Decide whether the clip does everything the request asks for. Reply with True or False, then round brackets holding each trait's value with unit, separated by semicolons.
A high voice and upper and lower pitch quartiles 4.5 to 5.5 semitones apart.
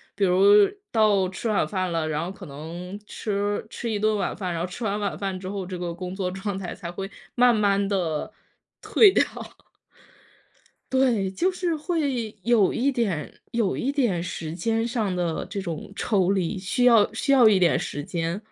False (200 Hz; 3.8 semitones)